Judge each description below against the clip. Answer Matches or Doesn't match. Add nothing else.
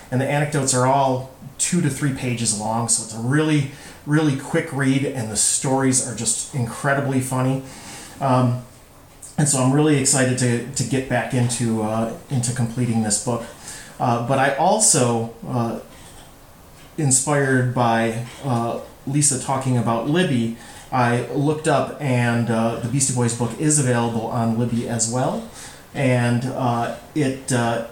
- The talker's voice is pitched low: Matches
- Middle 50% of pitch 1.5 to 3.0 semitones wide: Matches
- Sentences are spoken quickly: Doesn't match